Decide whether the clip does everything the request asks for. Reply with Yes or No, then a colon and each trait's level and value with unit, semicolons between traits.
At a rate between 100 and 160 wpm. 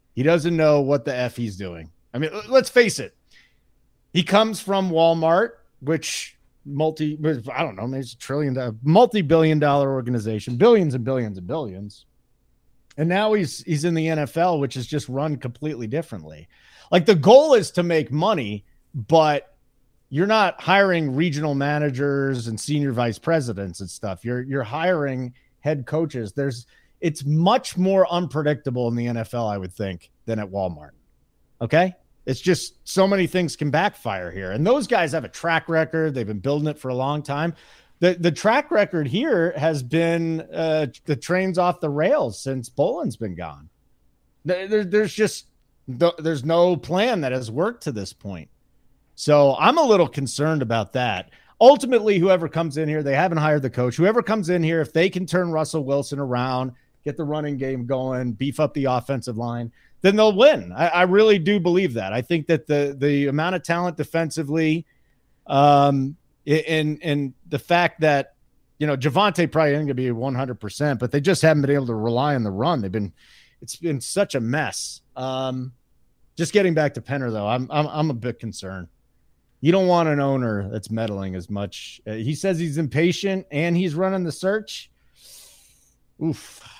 No: average, 180 wpm